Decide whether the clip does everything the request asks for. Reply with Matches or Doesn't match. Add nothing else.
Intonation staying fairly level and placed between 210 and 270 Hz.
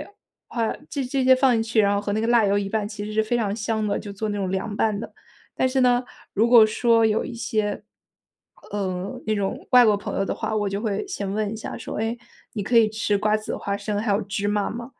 Matches